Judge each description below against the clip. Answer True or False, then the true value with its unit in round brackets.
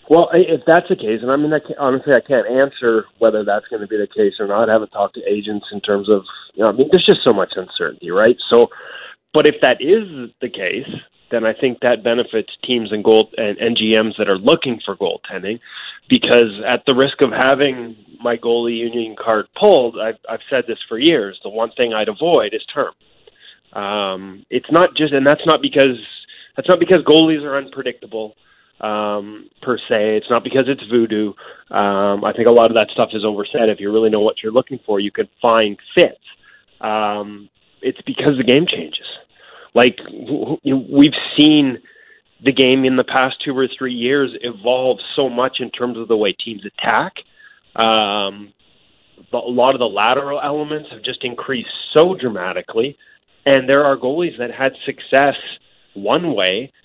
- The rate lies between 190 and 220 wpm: True (195 wpm)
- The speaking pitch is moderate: False (125 Hz)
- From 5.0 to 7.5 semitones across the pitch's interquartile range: True (5.3 semitones)